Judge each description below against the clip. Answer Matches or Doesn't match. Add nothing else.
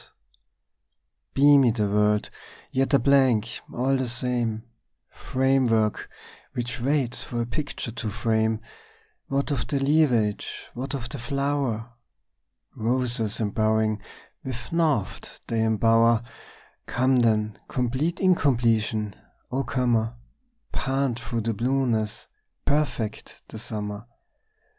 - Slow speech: Matches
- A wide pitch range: Doesn't match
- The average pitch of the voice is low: Matches